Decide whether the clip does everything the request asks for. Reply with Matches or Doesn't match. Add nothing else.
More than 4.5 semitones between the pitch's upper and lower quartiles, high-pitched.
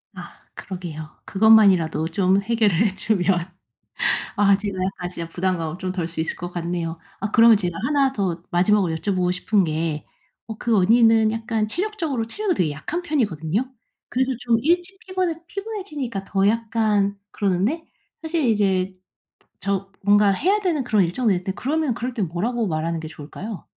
Matches